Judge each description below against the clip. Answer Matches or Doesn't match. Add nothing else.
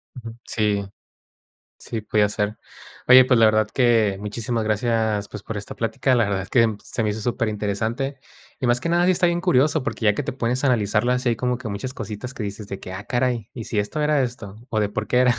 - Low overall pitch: Matches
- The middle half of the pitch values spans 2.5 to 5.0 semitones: Matches